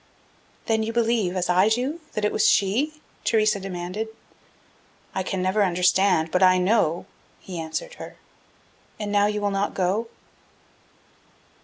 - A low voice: No, high, 200 Hz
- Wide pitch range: No, average, 3.2 semitones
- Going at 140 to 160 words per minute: Yes, average, 145 wpm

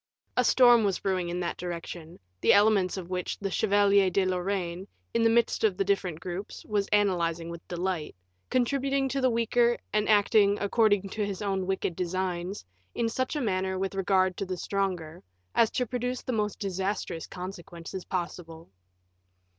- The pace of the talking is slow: No, average, 170 wpm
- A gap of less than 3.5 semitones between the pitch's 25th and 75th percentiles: Yes, average, 3.0 semitones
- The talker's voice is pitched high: Yes, high, 195 Hz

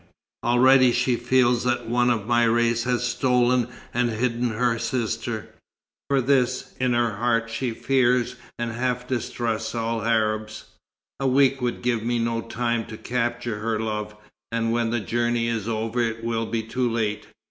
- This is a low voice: Yes, low, 120 Hz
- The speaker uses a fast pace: No, average, 165 wpm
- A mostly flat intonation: Yes, narrow, 1.4 semitones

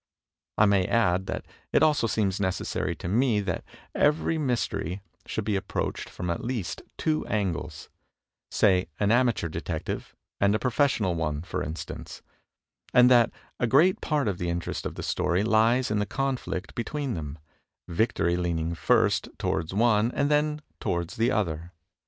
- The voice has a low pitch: Yes, low, 105 Hz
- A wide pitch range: Yes, wide, 5.7 semitones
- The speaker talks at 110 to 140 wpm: No, average, 165 wpm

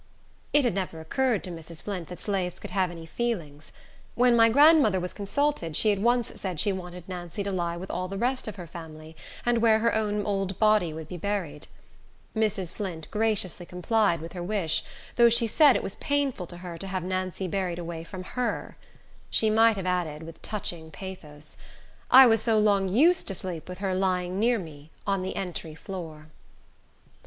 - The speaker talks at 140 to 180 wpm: No, average, 195 wpm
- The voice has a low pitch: No, high, 190 Hz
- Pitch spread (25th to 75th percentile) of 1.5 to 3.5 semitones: No, average, 4.1 semitones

